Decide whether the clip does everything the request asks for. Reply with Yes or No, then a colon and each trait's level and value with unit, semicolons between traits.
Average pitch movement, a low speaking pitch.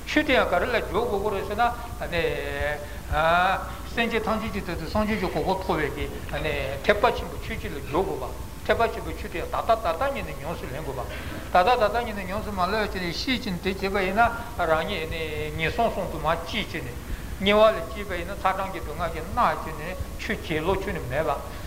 No: average, 3.7 semitones; high, 215 Hz